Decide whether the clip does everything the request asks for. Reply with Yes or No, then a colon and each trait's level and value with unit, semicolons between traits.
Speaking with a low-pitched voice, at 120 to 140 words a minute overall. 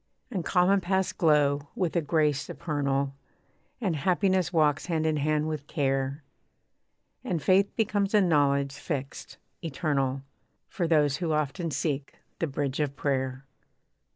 No: medium, 150 Hz; slow, 135 wpm